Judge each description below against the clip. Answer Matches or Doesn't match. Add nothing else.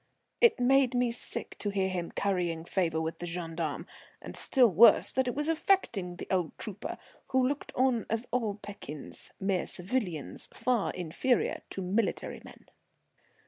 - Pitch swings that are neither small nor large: Doesn't match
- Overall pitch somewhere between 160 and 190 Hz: Doesn't match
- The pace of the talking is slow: Doesn't match